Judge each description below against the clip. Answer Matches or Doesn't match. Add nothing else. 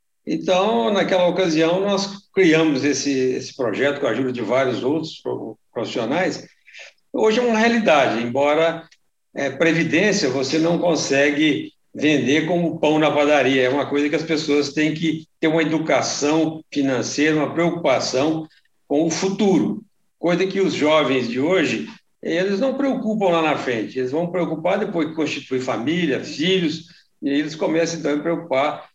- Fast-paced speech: Doesn't match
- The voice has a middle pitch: Matches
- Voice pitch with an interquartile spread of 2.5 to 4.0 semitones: Matches